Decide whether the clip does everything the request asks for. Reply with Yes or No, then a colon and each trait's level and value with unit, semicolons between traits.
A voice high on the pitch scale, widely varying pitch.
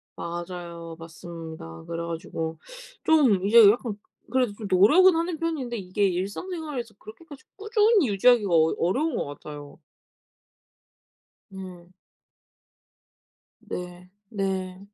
Yes: high, 195 Hz; wide, 7.1 semitones